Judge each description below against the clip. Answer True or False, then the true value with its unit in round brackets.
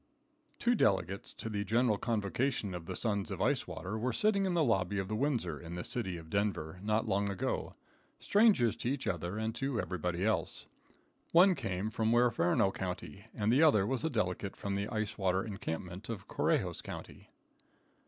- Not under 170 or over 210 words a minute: True (185 wpm)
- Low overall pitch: True (105 Hz)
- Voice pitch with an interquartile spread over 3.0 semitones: True (3.9 semitones)